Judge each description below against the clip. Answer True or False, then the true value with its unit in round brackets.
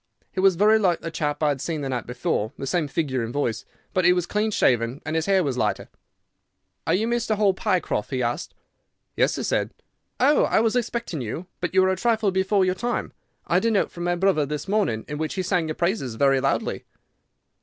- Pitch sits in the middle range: True (175 Hz)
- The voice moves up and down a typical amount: False (5.9 semitones)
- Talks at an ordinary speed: False (230 wpm)